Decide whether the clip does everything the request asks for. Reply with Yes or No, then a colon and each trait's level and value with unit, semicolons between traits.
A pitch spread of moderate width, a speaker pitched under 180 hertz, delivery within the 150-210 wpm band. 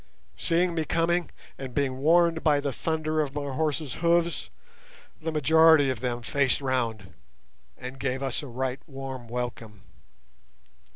No: average, 3.8 semitones; medium, 140 Hz; average, 140 wpm